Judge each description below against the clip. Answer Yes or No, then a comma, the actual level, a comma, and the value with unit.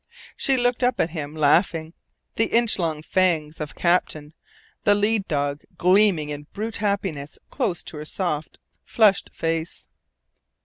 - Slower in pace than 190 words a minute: Yes, average, 140 wpm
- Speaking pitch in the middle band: Yes, medium, 170 Hz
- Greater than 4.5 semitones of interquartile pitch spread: Yes, average, 5.2 semitones